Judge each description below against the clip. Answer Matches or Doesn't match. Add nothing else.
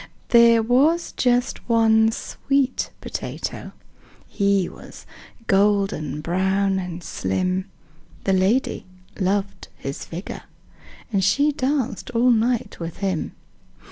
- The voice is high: Matches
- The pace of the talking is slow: Matches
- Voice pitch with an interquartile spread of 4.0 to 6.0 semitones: Matches